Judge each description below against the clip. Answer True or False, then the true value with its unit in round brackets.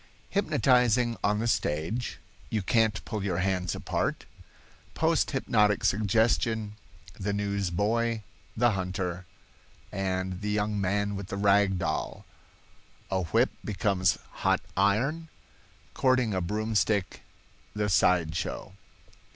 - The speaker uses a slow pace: True (95 wpm)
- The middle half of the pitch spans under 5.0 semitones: True (2.9 semitones)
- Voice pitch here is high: False (100 Hz)